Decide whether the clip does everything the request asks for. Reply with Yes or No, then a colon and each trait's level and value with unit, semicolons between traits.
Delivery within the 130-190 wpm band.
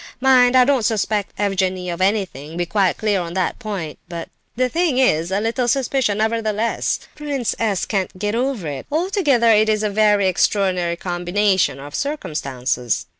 Yes: average, 165 wpm